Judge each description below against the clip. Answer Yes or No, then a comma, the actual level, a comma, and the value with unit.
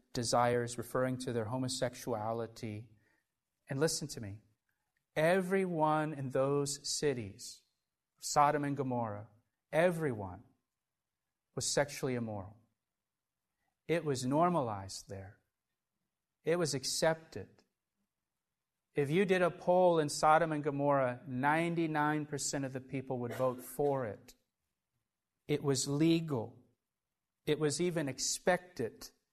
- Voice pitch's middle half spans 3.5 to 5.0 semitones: Yes, average, 4.2 semitones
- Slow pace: Yes, slow, 105 wpm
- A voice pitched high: No, medium, 140 Hz